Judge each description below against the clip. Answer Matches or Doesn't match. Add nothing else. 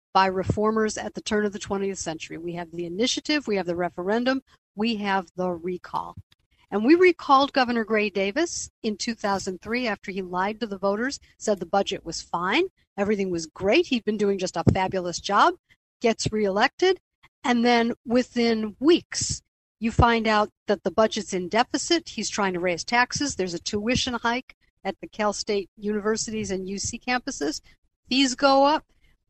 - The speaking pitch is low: Doesn't match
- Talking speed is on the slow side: Doesn't match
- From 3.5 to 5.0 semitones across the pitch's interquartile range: Matches